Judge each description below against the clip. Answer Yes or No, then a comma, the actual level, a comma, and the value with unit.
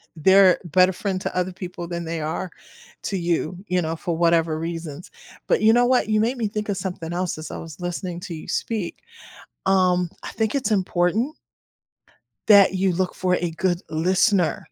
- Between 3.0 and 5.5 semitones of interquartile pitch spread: No, narrow, 2.6 semitones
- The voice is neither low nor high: Yes, medium, 180 Hz